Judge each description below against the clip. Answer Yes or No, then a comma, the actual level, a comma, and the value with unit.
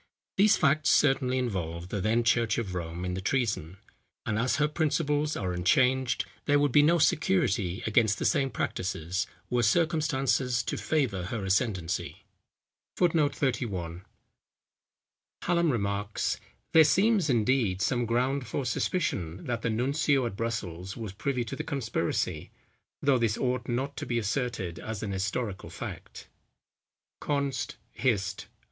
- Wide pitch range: Yes, wide, 6.0 semitones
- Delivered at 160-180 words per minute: No, average, 140 wpm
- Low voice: Yes, low, 120 Hz